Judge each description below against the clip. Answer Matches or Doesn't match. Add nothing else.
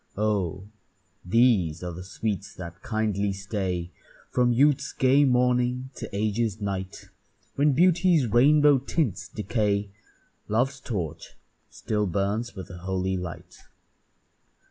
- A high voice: Doesn't match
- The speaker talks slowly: Matches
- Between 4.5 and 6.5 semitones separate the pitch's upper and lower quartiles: Matches